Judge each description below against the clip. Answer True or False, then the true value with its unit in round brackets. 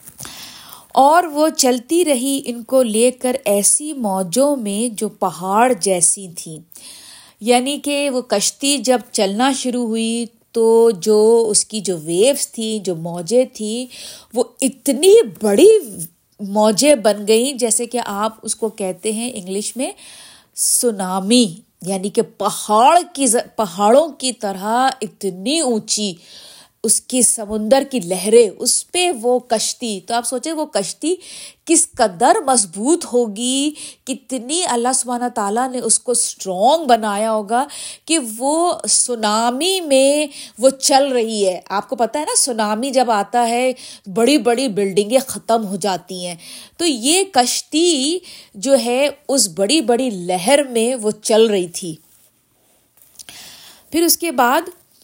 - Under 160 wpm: True (140 wpm)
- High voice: True (240 Hz)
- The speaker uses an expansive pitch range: False (4.4 semitones)